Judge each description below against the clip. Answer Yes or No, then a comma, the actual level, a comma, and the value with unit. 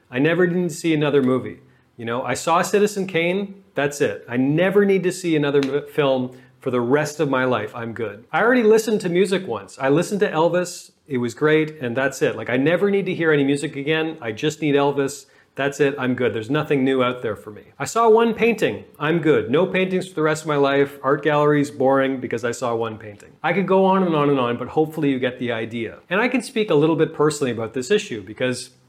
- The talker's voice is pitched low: No, medium, 150 Hz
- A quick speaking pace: Yes, fast, 245 wpm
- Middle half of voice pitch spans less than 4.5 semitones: No, wide, 5.5 semitones